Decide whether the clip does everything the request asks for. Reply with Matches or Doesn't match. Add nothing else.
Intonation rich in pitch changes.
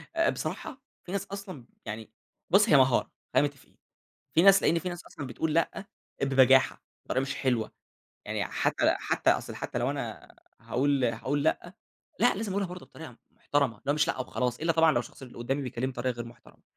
Matches